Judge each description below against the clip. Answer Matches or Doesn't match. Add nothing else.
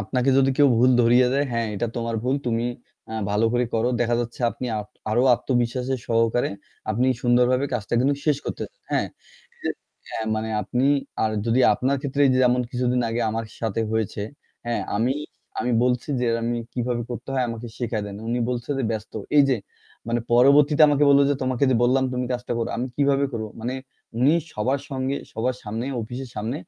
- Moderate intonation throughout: Doesn't match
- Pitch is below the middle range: Matches